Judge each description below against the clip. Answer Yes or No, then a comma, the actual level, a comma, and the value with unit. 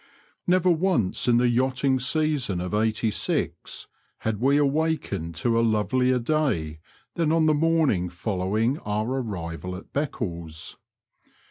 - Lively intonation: Yes, wide, 7.2 semitones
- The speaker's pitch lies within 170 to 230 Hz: No, low, 120 Hz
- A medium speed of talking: No, slow, 125 wpm